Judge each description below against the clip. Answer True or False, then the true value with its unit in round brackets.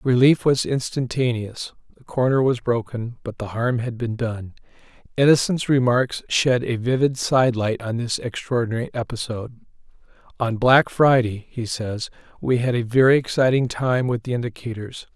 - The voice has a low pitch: True (120 Hz)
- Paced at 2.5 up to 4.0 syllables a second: False (4.9 syllables/s)